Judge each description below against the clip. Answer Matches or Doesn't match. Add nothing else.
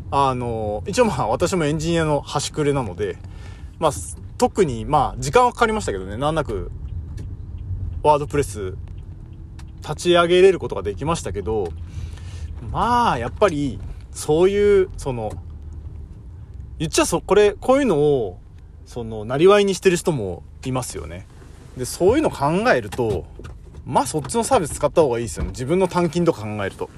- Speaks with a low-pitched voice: Matches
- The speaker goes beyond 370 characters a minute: Doesn't match